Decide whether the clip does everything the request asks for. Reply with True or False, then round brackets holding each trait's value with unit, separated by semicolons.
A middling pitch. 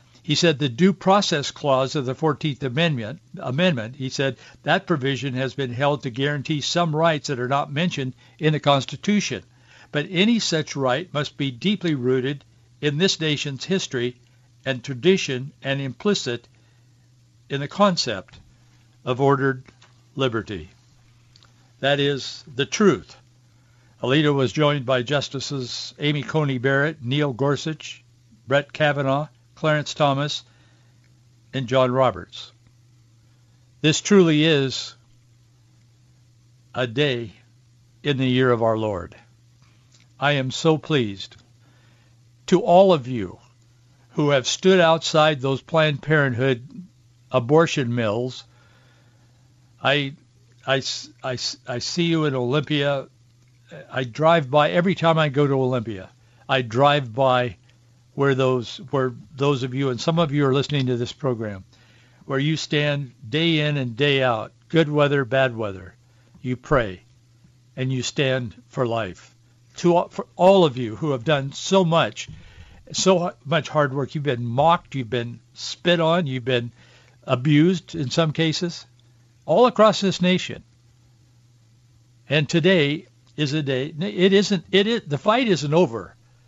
False (130 Hz)